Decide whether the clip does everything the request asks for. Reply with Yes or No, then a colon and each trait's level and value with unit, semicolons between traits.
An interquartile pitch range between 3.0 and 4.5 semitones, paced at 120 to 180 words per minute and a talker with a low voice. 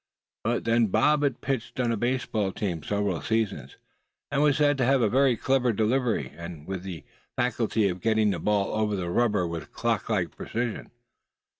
Yes: average, 4.1 semitones; average, 175 wpm; low, 110 Hz